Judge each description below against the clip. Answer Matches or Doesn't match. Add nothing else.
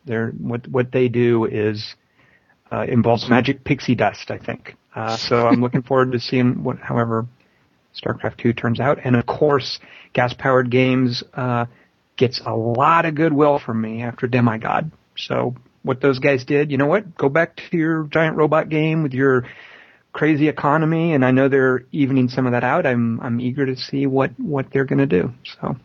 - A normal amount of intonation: Matches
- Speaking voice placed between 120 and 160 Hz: Matches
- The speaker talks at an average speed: Matches